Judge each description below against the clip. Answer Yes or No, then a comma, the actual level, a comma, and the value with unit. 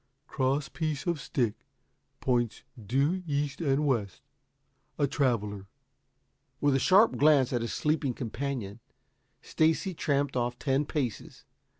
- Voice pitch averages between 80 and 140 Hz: Yes, low, 135 Hz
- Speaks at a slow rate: Yes, slow, 120 wpm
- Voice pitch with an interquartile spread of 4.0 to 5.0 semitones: No, average, 3.6 semitones